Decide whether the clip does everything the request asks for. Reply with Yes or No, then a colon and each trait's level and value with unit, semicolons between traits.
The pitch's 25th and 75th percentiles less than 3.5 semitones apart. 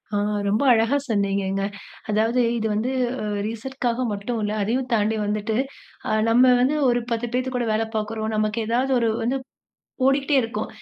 Yes: average, 2.8 semitones